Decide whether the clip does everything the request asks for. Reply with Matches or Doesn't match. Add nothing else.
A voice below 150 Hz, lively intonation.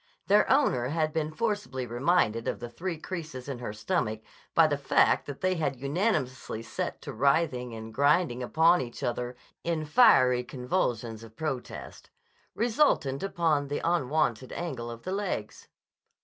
Matches